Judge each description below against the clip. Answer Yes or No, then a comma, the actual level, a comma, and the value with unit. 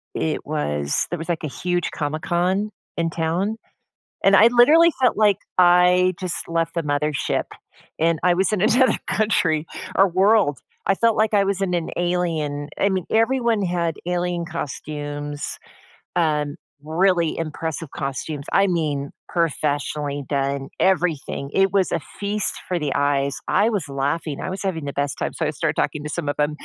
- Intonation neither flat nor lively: Yes, average, 4.6 semitones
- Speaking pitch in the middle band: Yes, medium, 170 Hz